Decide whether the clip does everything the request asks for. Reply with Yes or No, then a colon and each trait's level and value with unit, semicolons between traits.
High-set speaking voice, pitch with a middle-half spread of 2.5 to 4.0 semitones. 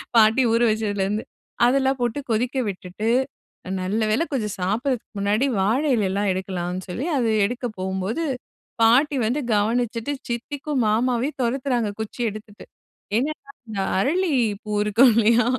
Yes: high, 225 Hz; average, 3.7 semitones